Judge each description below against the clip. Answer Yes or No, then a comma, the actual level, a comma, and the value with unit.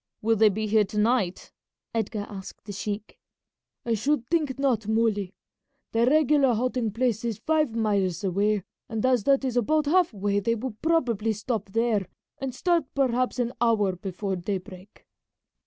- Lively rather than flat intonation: No, average, 3.8 semitones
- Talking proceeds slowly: No, average, 160 wpm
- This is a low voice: No, high, 225 Hz